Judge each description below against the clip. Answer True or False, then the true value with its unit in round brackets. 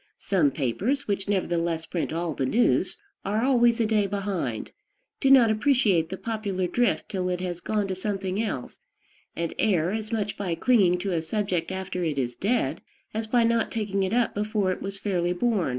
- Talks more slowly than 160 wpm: False (190 wpm)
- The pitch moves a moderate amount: True (3.8 semitones)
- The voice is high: True (195 Hz)